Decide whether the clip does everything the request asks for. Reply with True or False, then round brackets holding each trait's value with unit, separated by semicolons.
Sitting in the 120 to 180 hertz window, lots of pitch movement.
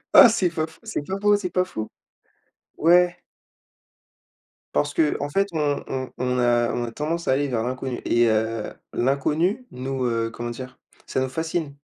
True (140 Hz; 6.2 semitones)